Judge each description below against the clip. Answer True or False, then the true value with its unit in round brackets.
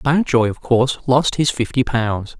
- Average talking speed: True (175 wpm)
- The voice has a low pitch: True (125 Hz)